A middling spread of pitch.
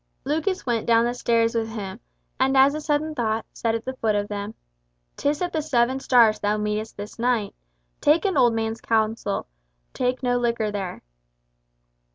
Yes: average, 3.4 semitones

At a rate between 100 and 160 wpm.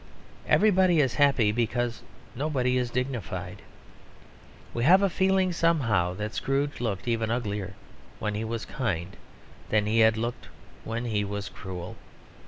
Yes: average, 140 wpm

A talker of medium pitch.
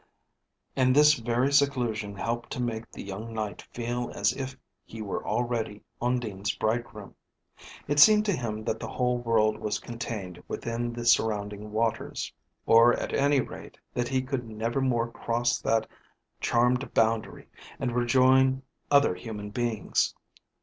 No: low, 120 Hz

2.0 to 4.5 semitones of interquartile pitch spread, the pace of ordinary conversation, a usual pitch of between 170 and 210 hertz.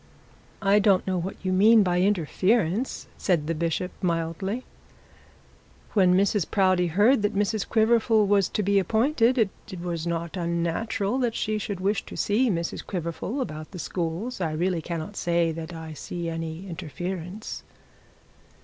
Yes: average, 3.7 semitones; average, 150 wpm; medium, 185 Hz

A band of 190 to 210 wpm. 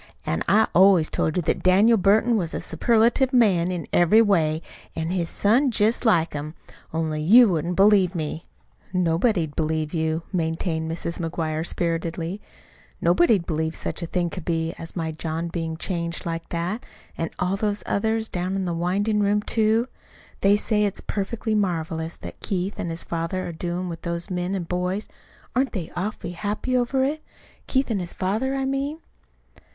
No: average, 175 wpm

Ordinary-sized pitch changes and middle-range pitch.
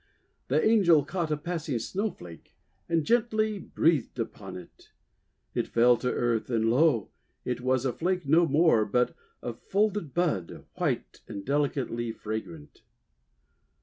No: wide, 6.4 semitones; medium, 145 Hz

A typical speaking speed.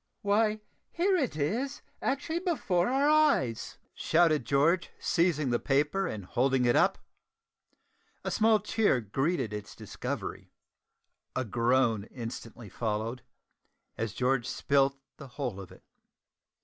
No: slow, 125 wpm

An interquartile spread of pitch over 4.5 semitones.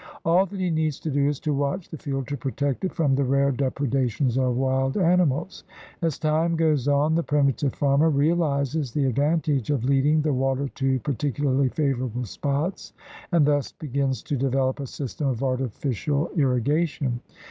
No: narrow, 2.6 semitones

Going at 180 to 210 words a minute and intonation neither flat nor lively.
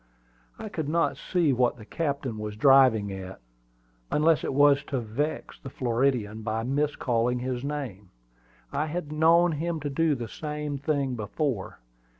No: average, 155 wpm; average, 4.5 semitones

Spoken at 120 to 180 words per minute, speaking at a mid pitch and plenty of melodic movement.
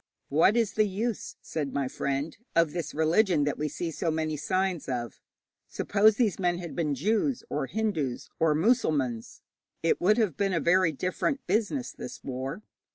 Yes: average, 170 wpm; medium, 170 Hz; wide, 6.0 semitones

